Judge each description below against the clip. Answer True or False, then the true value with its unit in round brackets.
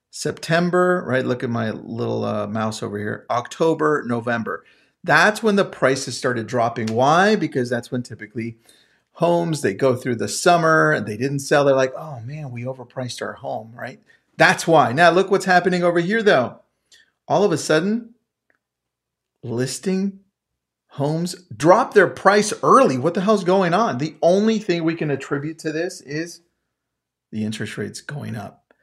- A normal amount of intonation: False (6.7 semitones)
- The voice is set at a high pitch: False (150 Hz)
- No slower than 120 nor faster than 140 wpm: False (165 wpm)